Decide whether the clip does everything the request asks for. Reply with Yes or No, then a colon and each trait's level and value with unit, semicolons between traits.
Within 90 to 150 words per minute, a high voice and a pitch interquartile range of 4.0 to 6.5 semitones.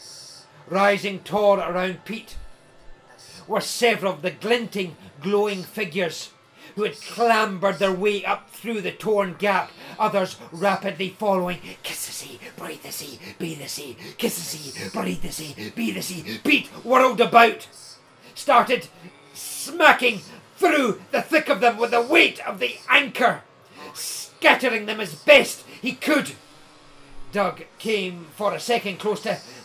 Yes: average, 140 wpm; high, 200 Hz; average, 4.3 semitones